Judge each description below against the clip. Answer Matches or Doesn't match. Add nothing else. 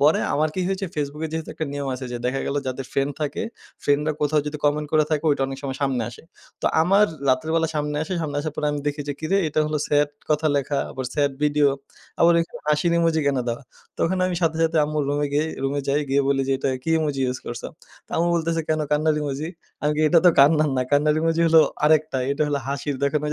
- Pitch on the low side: Doesn't match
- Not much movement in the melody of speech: Matches